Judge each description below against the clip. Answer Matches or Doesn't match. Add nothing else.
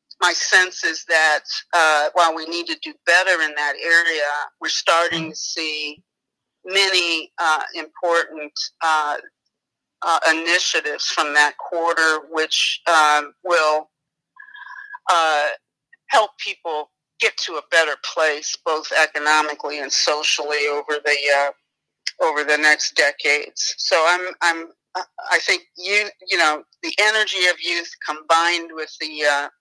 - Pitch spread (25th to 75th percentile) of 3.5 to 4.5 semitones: Doesn't match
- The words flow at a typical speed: Doesn't match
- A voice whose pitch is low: Doesn't match